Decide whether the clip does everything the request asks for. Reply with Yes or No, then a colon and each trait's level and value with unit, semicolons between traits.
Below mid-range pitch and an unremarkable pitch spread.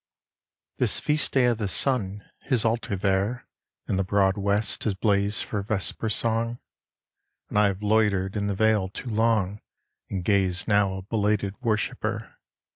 No: low, 105 Hz; narrow, 2.3 semitones